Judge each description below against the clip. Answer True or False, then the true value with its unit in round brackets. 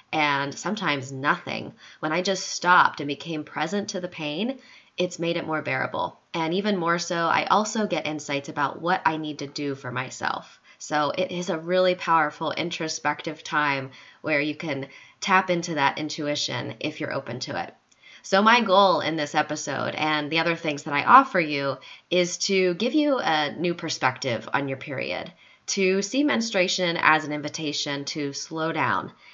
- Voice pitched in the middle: True (160 Hz)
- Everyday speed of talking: True (180 wpm)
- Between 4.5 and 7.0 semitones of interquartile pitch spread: False (3.8 semitones)